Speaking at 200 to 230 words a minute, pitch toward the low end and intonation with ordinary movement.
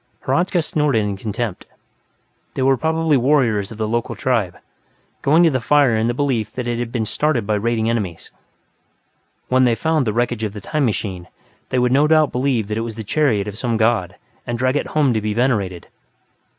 Yes: fast, 205 wpm; low, 120 Hz; average, 4.0 semitones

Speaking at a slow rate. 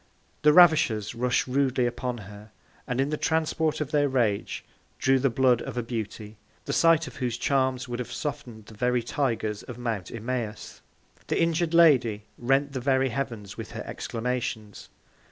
No: average, 170 wpm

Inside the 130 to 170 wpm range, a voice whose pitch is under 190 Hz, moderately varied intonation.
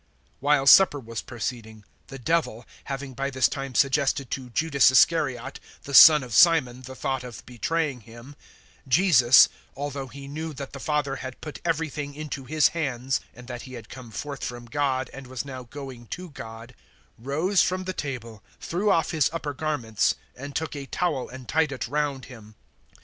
No: average, 185 wpm; low, 135 Hz; average, 3.2 semitones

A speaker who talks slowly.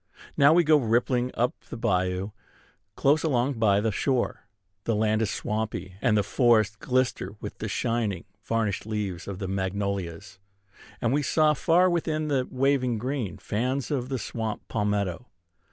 No: average, 155 wpm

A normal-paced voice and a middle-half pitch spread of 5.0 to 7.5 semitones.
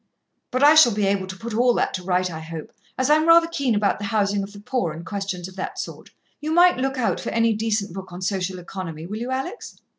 No: fast, 245 wpm; wide, 5.5 semitones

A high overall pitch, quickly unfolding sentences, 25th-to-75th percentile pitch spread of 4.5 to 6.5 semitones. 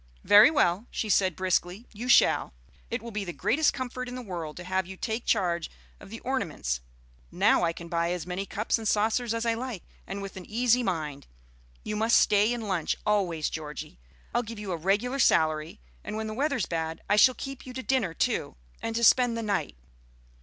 Yes: high, 210 Hz; fast, 210 wpm; average, 5.1 semitones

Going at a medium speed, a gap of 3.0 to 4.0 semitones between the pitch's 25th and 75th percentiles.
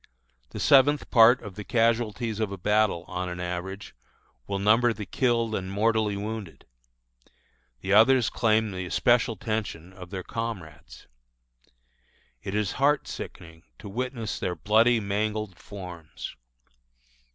No: slow, 130 wpm; average, 3.4 semitones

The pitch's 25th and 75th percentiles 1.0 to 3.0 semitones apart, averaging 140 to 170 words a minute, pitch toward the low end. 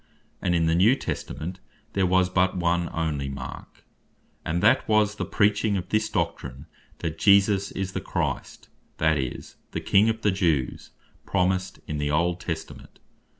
No: average, 3.5 semitones; average, 160 wpm; very low, 90 Hz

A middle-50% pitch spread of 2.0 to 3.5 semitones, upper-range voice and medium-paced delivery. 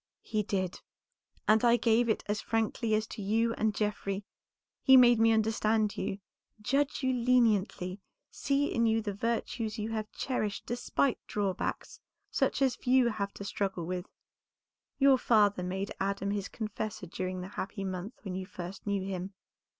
Yes: average, 2.9 semitones; high, 215 Hz; average, 160 wpm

